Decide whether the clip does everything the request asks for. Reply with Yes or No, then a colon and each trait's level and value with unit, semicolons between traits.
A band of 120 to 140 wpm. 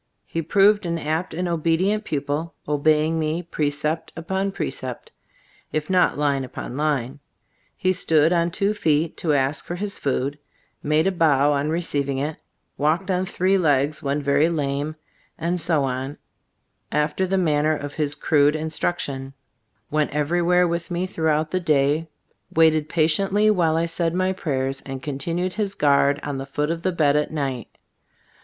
No: average, 160 wpm